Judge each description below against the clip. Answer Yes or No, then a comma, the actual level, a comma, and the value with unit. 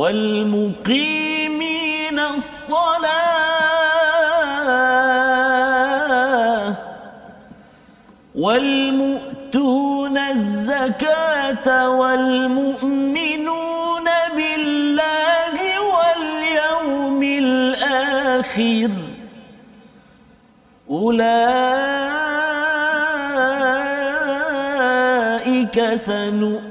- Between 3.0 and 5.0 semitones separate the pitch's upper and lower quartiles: Yes, average, 3.4 semitones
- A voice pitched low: No, very high, 275 Hz